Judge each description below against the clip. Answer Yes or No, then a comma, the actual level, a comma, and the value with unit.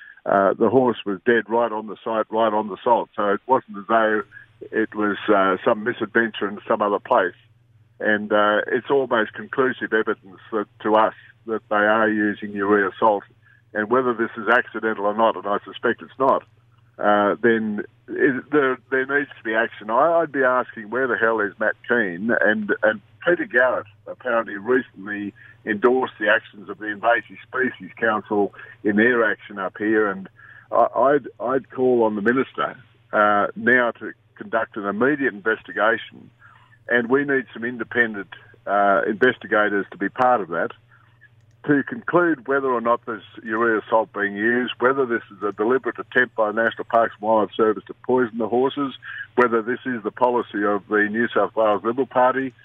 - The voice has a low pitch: Yes, low, 115 Hz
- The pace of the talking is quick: No, average, 180 wpm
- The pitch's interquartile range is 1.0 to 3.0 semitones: Yes, narrow, 2.5 semitones